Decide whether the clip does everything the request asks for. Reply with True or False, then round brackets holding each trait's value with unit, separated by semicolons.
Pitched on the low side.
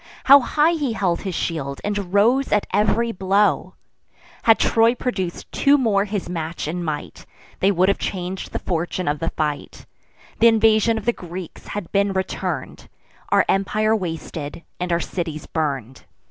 False (190 Hz)